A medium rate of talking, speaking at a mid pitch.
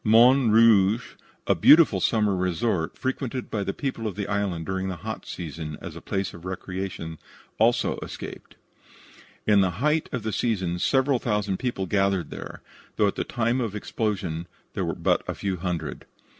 No: average, 175 wpm; low, 100 Hz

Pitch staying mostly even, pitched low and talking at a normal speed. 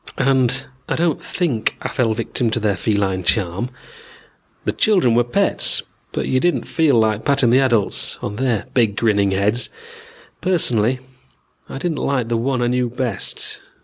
No: average, 3.7 semitones; low, 120 Hz; average, 155 wpm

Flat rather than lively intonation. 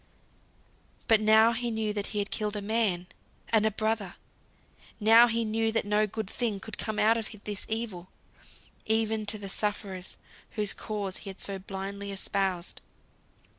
Yes: narrow, 1.9 semitones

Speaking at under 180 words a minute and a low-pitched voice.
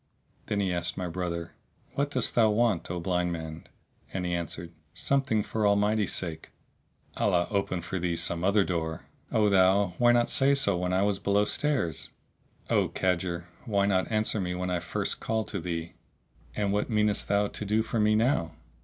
No: average, 190 wpm; low, 100 Hz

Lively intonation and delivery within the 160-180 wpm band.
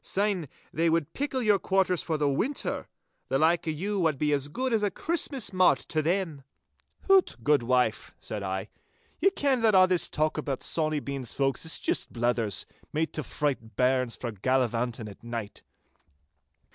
Yes: wide, 6.9 semitones; average, 170 wpm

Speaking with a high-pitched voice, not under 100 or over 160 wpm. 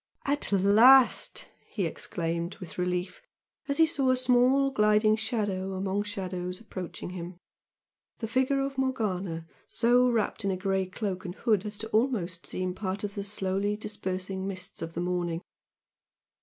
Yes: high, 200 Hz; average, 155 wpm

